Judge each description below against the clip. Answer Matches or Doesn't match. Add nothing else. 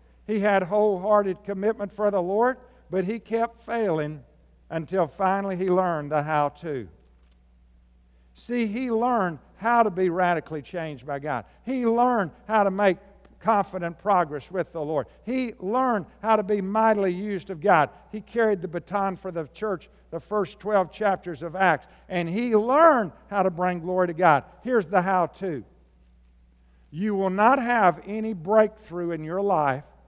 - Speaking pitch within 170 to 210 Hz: Matches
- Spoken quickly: Doesn't match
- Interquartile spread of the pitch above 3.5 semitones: Matches